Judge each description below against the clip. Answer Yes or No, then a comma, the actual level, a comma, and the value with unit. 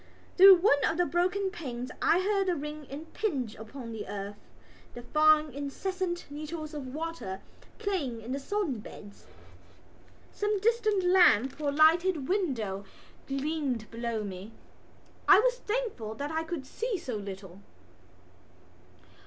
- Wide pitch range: Yes, wide, 7.5 semitones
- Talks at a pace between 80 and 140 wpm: Yes, slow, 135 wpm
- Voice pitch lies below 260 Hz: No, very high, 300 Hz